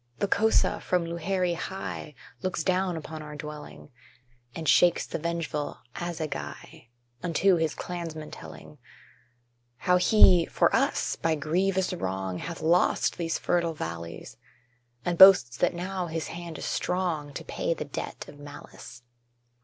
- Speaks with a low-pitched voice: No, medium, 165 Hz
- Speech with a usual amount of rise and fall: Yes, average, 3.1 semitones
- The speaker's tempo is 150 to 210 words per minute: No, average, 140 wpm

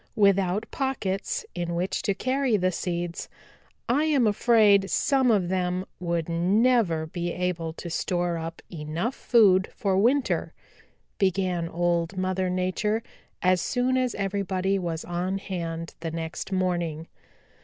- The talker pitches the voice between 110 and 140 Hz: No, medium, 185 Hz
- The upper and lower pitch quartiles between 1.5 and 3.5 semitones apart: Yes, average, 3.2 semitones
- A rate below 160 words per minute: Yes, slow, 135 wpm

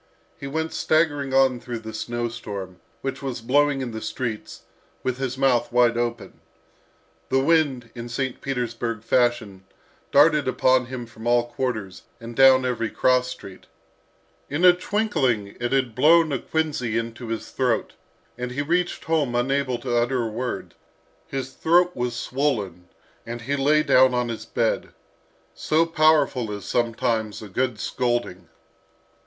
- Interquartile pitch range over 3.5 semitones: No, average, 2.9 semitones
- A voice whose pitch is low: Yes, low, 125 Hz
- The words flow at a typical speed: Yes, average, 150 wpm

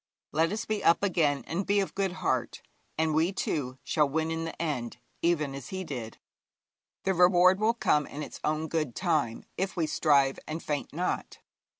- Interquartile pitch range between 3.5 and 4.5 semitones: Yes, average, 3.8 semitones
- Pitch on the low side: No, medium, 160 Hz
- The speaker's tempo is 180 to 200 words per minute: Yes, average, 190 wpm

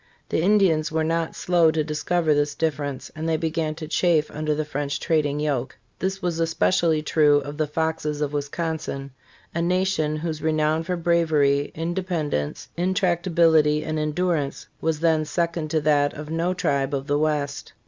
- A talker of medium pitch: Yes, medium, 155 Hz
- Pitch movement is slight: Yes, narrow, 2.0 semitones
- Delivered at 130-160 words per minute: No, average, 170 wpm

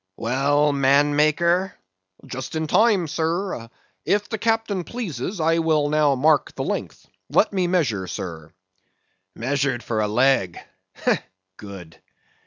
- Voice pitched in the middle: Yes, medium, 150 Hz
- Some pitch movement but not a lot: No, wide, 5.7 semitones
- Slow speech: Yes, slow, 125 wpm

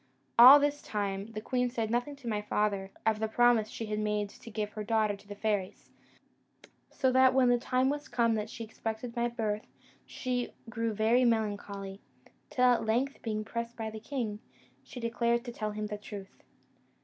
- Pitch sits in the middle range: No, high, 225 Hz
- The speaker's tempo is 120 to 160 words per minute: No, average, 185 wpm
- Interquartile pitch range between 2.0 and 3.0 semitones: Yes, narrow, 2.5 semitones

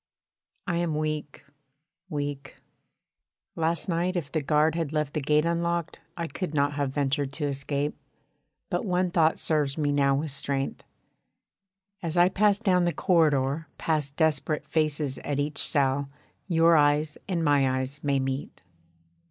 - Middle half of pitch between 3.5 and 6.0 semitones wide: No, average, 2.8 semitones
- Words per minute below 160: Yes, average, 150 wpm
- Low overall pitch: No, medium, 150 Hz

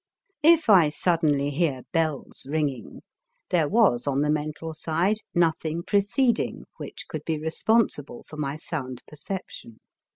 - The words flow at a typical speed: No, slow, 130 wpm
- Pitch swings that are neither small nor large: Yes, average, 3.6 semitones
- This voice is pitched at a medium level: Yes, medium, 155 Hz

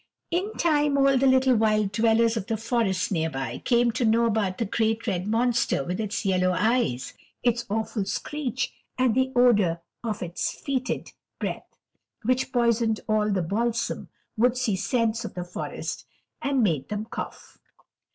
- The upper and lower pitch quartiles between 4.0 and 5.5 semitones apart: No, average, 3.5 semitones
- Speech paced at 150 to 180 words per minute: Yes, average, 160 wpm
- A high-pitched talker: Yes, high, 225 Hz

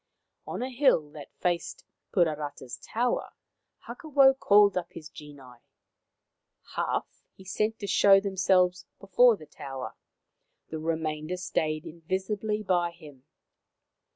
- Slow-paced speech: Yes, slow, 120 wpm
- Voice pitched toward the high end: No, medium, 180 Hz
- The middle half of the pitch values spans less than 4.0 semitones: No, average, 4.7 semitones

